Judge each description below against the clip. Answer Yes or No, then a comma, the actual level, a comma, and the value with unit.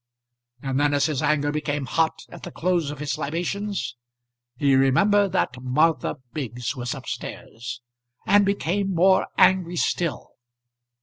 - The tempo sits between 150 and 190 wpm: No, average, 140 wpm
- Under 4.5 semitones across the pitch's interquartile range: No, average, 5.1 semitones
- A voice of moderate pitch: Yes, medium, 150 Hz